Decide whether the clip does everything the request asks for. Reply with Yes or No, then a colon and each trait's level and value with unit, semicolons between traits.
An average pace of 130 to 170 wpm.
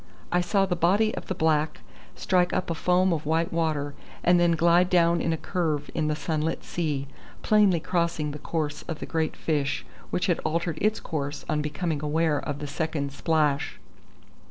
No: average, 185 wpm